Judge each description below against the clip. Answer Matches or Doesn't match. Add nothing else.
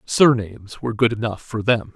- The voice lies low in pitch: Matches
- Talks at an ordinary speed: Matches